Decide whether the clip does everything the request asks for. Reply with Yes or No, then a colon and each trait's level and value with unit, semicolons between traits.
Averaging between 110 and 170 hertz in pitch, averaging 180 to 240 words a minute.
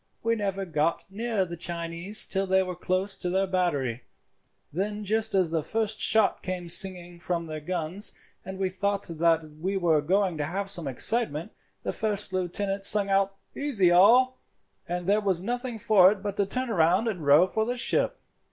No: high, 190 Hz; average, 190 wpm